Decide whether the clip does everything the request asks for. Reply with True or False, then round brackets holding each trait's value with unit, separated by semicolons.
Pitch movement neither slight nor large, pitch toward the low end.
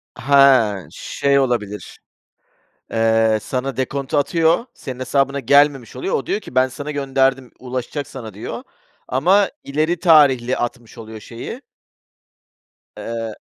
True (3.4 semitones; 130 Hz)